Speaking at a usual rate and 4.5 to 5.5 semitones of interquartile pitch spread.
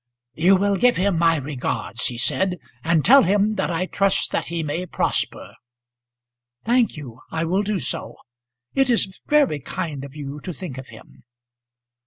Yes: average, 170 wpm; average, 5.2 semitones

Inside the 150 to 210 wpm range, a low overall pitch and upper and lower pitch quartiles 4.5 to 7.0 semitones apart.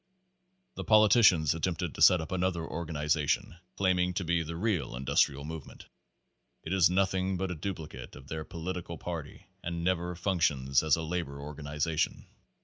No: average, 155 wpm; very low, 85 Hz; average, 3.2 semitones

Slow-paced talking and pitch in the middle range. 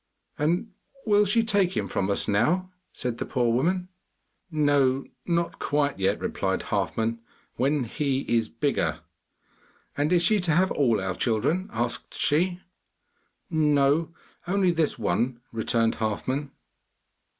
Yes: slow, 130 wpm; medium, 145 Hz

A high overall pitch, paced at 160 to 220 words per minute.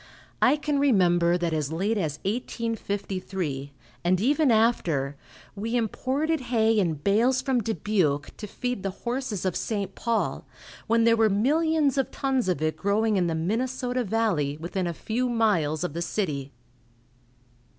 No: high, 215 Hz; average, 150 wpm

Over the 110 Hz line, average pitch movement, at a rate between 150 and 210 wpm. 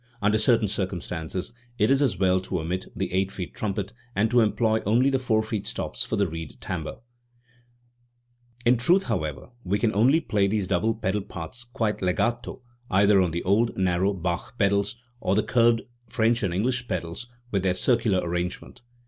No: low, 100 Hz; average, 3.8 semitones; average, 180 wpm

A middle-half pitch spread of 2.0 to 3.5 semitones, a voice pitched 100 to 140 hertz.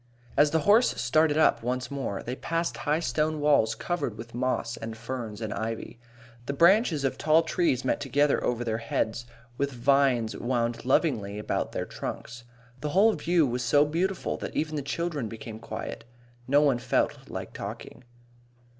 No: average, 4.8 semitones; low, 135 Hz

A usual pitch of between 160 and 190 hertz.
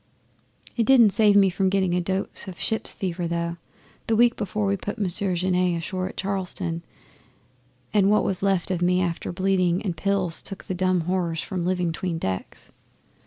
Yes: medium, 185 Hz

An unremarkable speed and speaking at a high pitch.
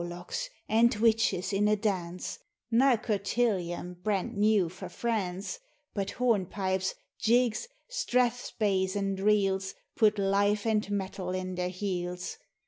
No: slow, 120 wpm; high, 200 Hz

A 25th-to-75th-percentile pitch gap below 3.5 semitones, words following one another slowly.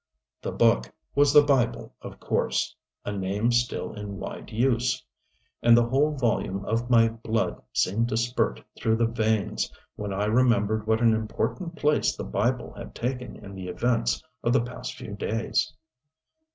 No: average, 2.8 semitones; average, 165 wpm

